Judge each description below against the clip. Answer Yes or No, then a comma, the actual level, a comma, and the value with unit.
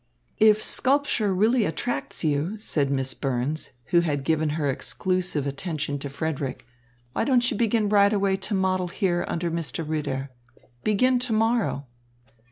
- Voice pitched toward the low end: No, medium, 175 Hz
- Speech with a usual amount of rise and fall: No, wide, 6.5 semitones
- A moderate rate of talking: Yes, average, 150 wpm